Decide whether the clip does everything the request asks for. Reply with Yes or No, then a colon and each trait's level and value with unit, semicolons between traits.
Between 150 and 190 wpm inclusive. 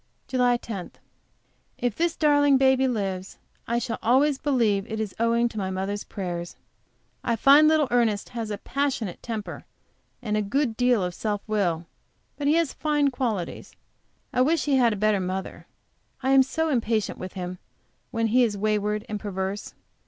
Yes: average, 170 wpm